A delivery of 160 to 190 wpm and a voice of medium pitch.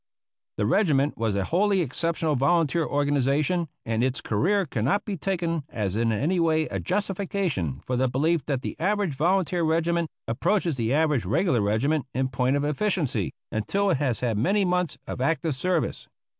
Yes: average, 170 wpm; medium, 150 Hz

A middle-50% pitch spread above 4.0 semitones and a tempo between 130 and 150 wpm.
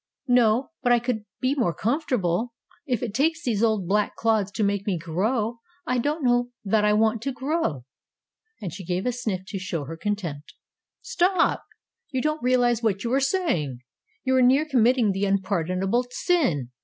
No: average, 4.8 semitones; average, 180 wpm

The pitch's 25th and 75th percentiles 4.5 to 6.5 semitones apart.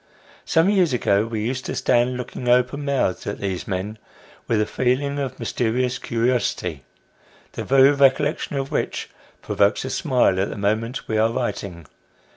No: average, 4.0 semitones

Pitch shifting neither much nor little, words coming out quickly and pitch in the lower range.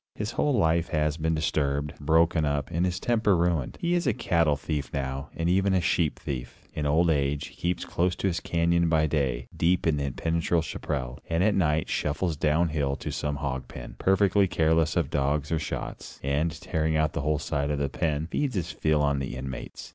Yes: average, 3.0 semitones; fast, 210 wpm; very low, 80 Hz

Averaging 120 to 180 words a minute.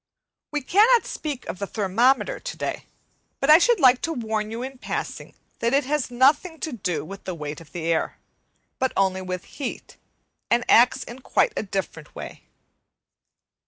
Yes: average, 170 wpm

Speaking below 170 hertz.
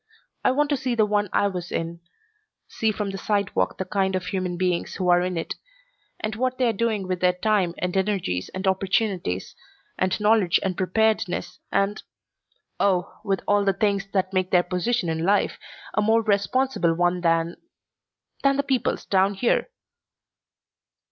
No: high, 195 Hz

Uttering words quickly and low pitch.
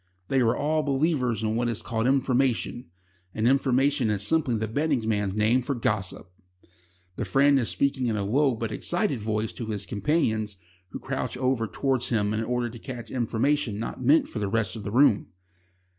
No: average, 190 wpm; low, 120 Hz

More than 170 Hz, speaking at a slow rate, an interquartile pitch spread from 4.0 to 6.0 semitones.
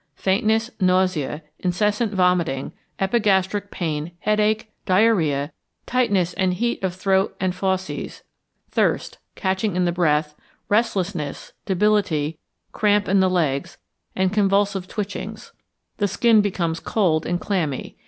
No: high, 190 Hz; slow, 115 wpm; average, 3.0 semitones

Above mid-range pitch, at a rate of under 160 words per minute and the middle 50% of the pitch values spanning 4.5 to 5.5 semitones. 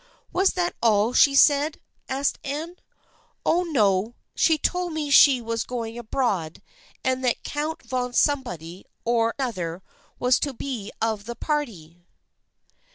Yes: very high, 250 Hz; average, 150 wpm; average, 4.9 semitones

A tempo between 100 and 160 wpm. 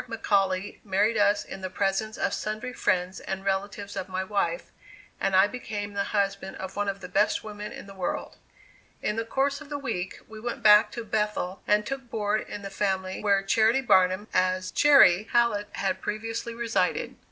No: average, 185 wpm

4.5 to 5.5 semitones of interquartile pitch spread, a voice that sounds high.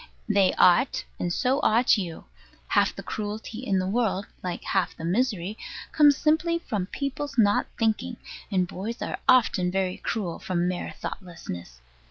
Yes: average, 5.2 semitones; high, 205 Hz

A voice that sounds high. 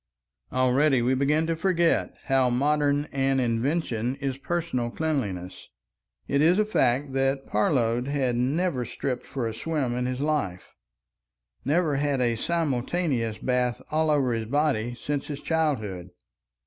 No: low, 135 Hz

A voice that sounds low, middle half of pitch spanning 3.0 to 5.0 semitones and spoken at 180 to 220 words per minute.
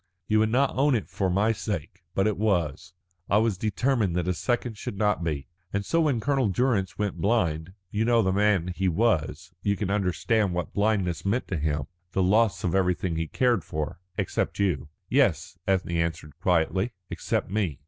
Yes: very low, 95 Hz; average, 4.2 semitones; average, 190 wpm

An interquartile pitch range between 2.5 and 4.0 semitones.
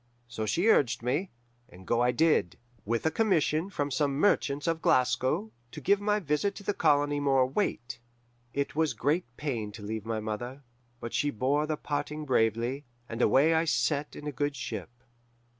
No: average, 4.5 semitones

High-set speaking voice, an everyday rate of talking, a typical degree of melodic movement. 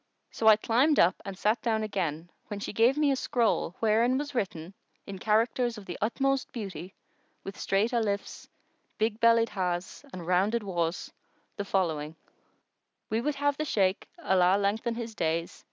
Yes: high, 210 Hz; average, 160 wpm; average, 4.0 semitones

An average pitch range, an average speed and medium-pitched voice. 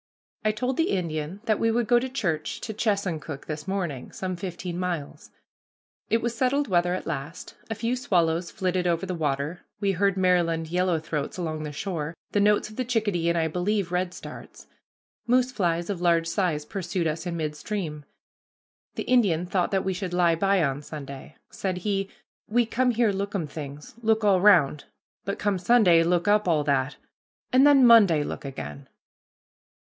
Yes: average, 4.3 semitones; average, 175 wpm; medium, 180 Hz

